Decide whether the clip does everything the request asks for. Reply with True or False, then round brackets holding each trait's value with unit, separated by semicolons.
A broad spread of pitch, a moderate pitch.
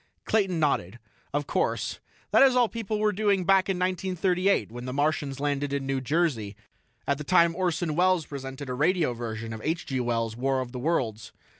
True (6.2 semitones; 145 Hz)